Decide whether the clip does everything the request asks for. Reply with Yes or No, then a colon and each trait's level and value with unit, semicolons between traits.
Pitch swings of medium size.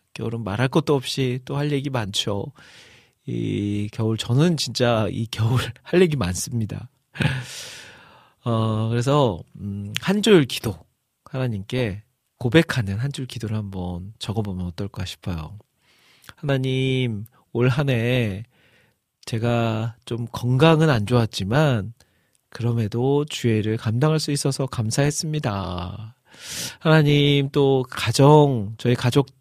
Yes: average, 3.8 semitones